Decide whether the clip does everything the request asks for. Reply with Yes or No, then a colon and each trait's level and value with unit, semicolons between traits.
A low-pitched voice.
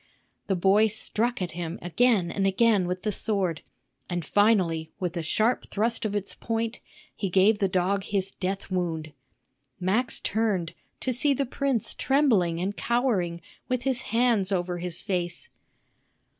No: high, 195 Hz